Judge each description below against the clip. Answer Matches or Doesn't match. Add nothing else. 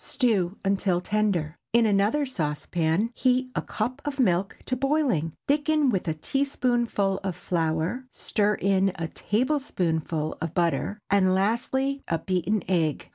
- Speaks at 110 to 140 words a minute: Matches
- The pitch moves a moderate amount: Doesn't match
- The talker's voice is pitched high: Matches